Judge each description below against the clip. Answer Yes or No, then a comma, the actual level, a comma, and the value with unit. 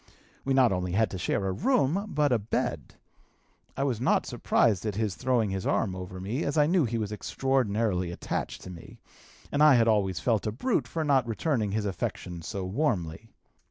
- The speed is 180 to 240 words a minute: Yes, average, 195 wpm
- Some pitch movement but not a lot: No, wide, 5.8 semitones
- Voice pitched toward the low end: Yes, low, 110 Hz